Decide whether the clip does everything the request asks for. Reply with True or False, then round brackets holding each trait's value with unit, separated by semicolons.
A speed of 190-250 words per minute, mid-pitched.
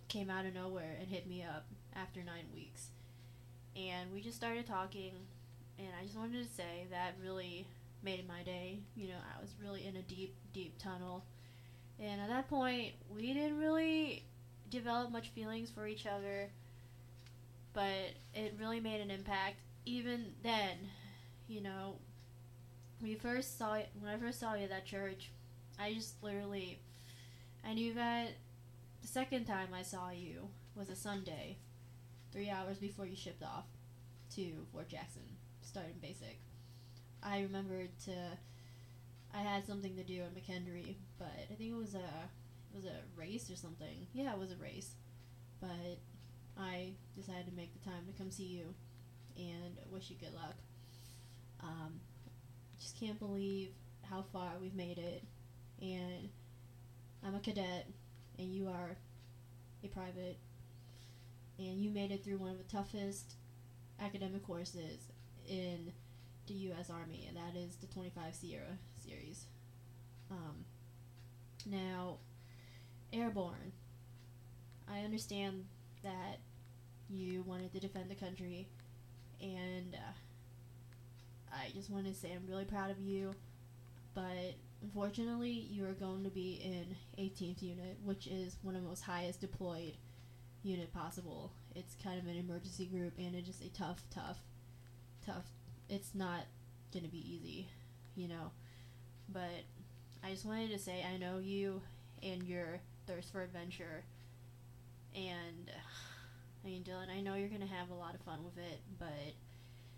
False (150 wpm; 175 Hz)